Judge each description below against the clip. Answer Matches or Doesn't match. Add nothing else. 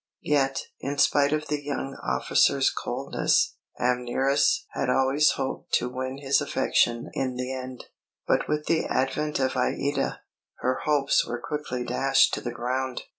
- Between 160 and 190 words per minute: Doesn't match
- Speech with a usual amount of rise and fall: Doesn't match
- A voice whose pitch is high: Doesn't match